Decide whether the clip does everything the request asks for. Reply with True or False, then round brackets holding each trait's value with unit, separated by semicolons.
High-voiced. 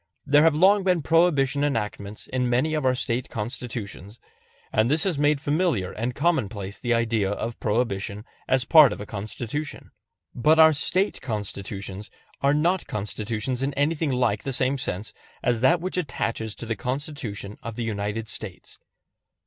False (125 Hz)